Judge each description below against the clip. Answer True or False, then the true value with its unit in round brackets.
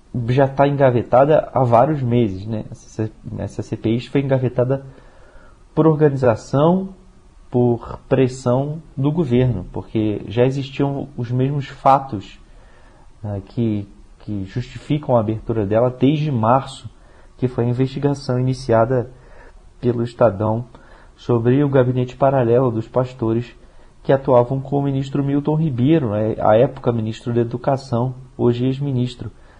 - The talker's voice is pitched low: True (125 Hz)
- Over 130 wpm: False (120 wpm)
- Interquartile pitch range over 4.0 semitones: False (3.2 semitones)